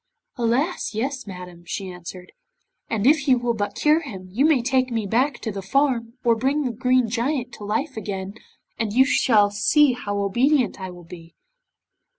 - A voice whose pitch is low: No, high, 235 Hz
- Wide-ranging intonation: No, average, 4.8 semitones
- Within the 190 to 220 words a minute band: No, average, 180 wpm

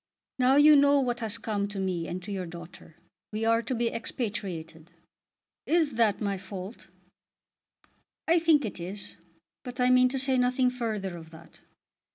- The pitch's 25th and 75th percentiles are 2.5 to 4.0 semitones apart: No, average, 5.1 semitones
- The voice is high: Yes, high, 225 Hz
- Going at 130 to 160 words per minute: No, average, 170 wpm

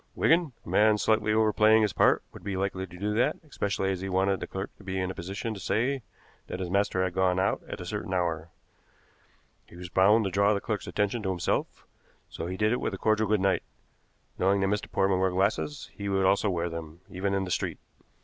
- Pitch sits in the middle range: No, very low, 95 Hz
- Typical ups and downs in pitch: No, narrow, 2.3 semitones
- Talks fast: Yes, fast, 230 wpm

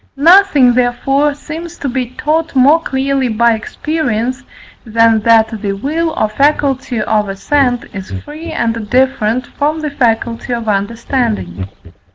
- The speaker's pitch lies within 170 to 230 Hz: No, very high, 250 Hz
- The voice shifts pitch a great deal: No, average, 4.4 semitones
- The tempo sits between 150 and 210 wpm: No, slow, 135 wpm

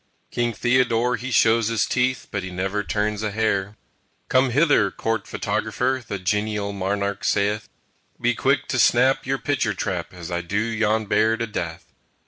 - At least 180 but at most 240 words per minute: No, average, 165 wpm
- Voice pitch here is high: No, low, 110 Hz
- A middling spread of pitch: Yes, average, 3.2 semitones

